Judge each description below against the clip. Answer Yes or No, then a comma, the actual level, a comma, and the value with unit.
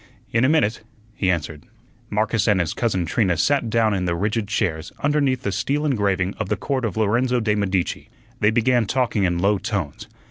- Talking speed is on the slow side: No, average, 190 wpm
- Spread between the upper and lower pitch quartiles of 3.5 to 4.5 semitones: Yes, average, 4.2 semitones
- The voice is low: Yes, low, 105 Hz